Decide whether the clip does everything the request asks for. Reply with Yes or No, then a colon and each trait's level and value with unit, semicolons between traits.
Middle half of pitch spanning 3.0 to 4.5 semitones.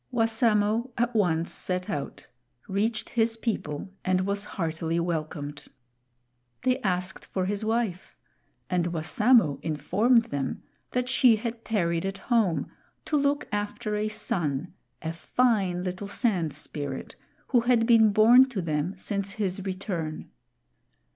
No: average, 4.9 semitones